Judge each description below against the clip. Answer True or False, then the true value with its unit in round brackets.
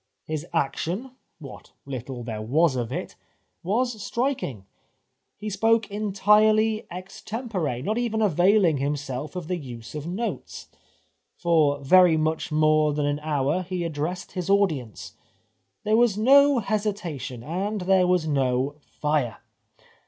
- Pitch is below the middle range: False (170 Hz)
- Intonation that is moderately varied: False (6.4 semitones)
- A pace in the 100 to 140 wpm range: True (135 wpm)